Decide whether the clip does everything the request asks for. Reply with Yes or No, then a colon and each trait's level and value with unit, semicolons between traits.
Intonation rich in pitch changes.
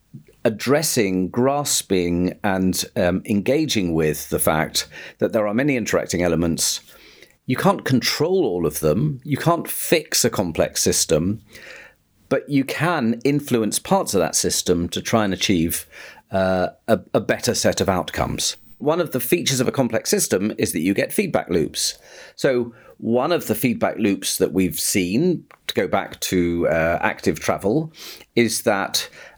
Yes: wide, 6.9 semitones